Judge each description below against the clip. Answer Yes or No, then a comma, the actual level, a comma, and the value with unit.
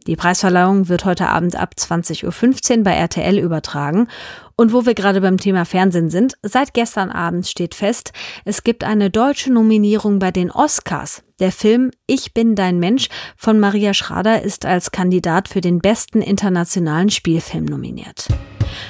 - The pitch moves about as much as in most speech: Yes, average, 3.7 semitones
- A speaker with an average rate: Yes, average, 160 wpm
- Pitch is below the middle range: No, high, 195 Hz